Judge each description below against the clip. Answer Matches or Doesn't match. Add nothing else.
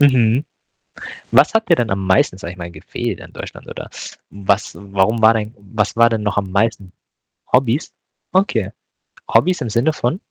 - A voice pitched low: Matches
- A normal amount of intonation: Matches